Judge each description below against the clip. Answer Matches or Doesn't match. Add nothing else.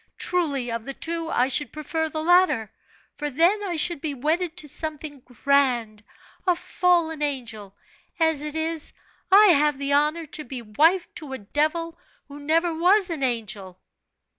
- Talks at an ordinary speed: Matches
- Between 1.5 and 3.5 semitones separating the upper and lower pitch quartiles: Doesn't match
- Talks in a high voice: Matches